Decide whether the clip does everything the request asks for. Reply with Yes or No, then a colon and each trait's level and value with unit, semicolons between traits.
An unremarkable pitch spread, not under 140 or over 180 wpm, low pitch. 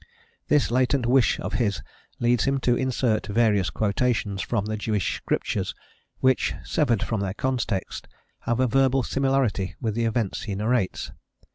Yes: average, 3.7 semitones; average, 150 wpm; low, 115 Hz